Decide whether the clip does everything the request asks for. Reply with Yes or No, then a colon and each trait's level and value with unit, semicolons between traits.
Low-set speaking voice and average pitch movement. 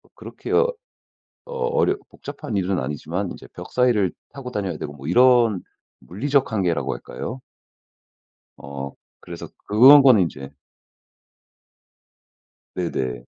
No: low, 105 Hz; wide, 8.1 semitones